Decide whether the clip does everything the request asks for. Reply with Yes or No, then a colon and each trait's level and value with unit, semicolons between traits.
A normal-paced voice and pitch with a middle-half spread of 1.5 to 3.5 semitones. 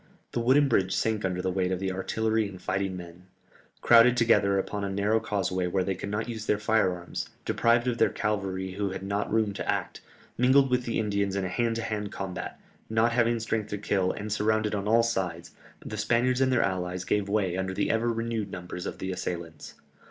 No: fast, 215 wpm; average, 3.2 semitones